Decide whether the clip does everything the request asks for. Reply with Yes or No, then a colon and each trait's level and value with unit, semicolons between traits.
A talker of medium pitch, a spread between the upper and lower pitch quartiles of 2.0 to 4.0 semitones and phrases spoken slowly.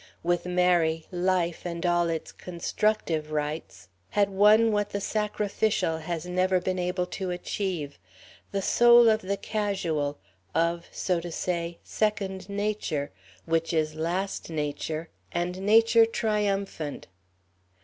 Yes: medium, 180 Hz; average, 3.6 semitones; slow, 125 wpm